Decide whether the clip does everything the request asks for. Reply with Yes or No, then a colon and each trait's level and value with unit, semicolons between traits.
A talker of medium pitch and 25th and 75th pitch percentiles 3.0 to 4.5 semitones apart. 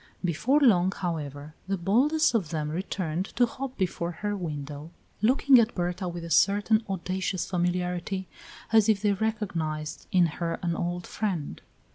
Yes: medium, 180 Hz; average, 3.9 semitones